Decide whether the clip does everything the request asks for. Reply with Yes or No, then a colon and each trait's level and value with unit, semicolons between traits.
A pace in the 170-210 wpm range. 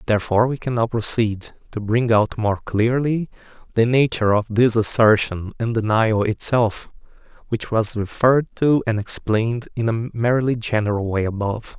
No: average, 155 wpm